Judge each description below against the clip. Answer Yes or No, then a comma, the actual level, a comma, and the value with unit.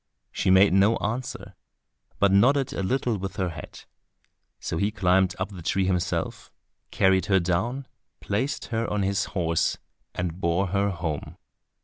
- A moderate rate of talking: Yes, average, 150 wpm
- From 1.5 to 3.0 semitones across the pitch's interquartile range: Yes, narrow, 2.6 semitones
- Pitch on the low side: Yes, very low, 95 Hz